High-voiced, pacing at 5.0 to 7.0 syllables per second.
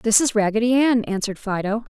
Yes: high, 220 Hz; 6.0 syllables/s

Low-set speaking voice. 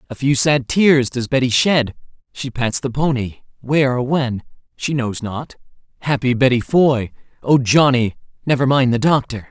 Yes: low, 130 Hz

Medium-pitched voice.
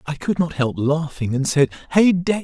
Yes: medium, 155 Hz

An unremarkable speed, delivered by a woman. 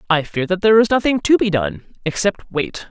No: fast, 225 wpm; female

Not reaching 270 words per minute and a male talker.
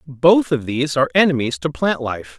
Yes: average, 200 wpm; male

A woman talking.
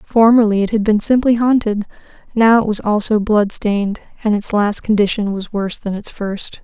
Yes: female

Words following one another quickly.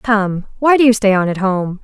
Yes: fast, 260 wpm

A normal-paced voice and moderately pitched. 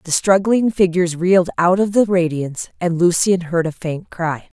Yes: average, 185 wpm; medium, 175 Hz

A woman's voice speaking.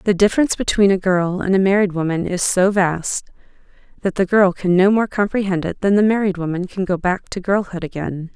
Yes: female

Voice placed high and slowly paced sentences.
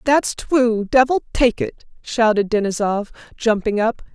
Yes: high, 230 Hz; slow, 130 wpm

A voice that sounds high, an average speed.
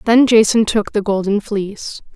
Yes: high, 210 Hz; average, 165 wpm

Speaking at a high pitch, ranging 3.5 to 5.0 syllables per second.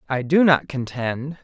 No: medium, 140 Hz; 4.2 syllables/s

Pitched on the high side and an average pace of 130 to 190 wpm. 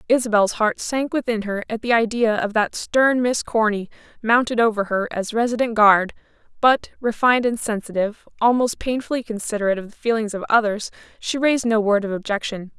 Yes: high, 225 Hz; average, 175 wpm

